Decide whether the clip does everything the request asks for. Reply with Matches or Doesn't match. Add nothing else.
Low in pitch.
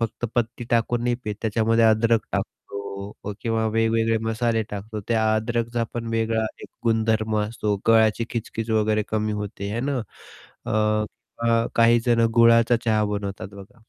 Matches